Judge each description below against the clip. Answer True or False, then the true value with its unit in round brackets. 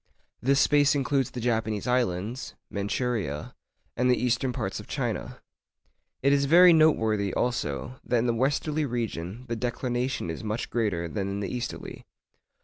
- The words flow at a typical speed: True (150 wpm)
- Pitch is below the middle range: True (120 Hz)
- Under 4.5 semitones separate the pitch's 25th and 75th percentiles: True (3.8 semitones)